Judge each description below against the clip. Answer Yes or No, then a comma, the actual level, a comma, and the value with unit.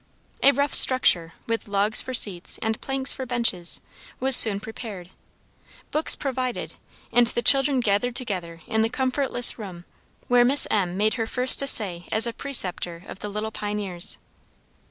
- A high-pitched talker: Yes, high, 225 Hz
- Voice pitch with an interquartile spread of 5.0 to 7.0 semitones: No, average, 4.4 semitones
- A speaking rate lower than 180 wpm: Yes, average, 155 wpm